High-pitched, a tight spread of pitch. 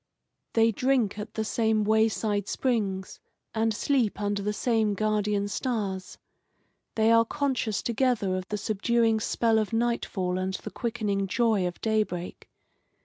Yes: high, 215 Hz; narrow, 2.2 semitones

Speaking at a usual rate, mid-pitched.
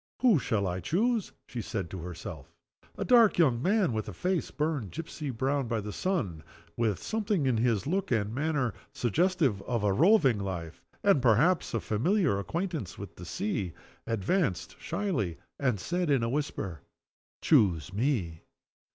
No: average, 160 wpm; low, 125 Hz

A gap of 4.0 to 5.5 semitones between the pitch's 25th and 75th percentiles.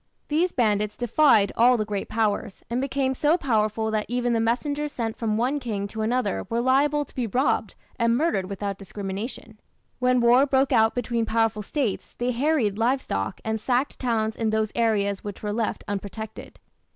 No: average, 3.2 semitones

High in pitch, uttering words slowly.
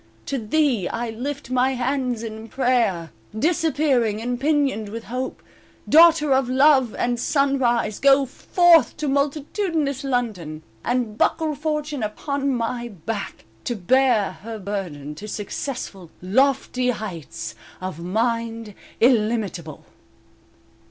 Yes: high, 245 Hz; slow, 115 wpm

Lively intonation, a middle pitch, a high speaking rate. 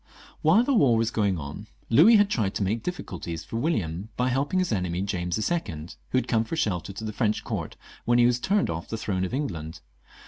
No: wide, 7.0 semitones; low, 110 Hz; fast, 220 wpm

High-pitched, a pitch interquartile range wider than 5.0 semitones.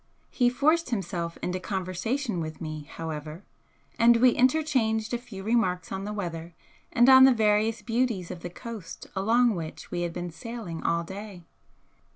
Yes: high, 205 Hz; wide, 5.4 semitones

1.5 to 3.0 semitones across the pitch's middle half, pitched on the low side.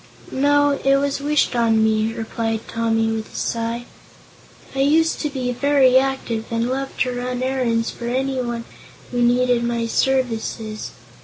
No: average, 2.7 semitones; high, 245 Hz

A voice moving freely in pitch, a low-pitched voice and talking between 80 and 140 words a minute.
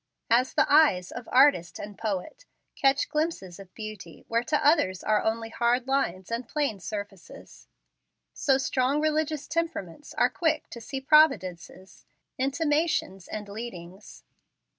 No: wide, 6.8 semitones; high, 240 Hz; slow, 135 wpm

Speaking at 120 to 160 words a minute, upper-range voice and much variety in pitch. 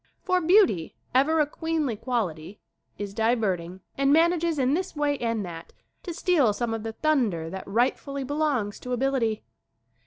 Yes: average, 155 wpm; very high, 250 Hz; wide, 6.7 semitones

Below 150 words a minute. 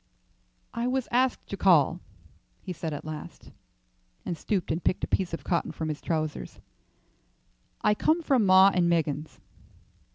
No: average, 155 wpm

